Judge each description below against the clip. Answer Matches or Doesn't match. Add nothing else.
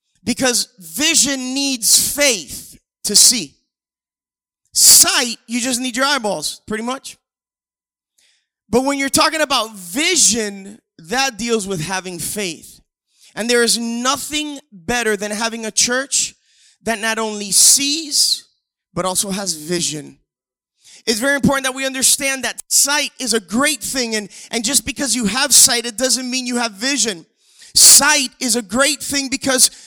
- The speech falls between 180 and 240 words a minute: Doesn't match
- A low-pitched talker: Doesn't match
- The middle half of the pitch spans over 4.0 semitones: Matches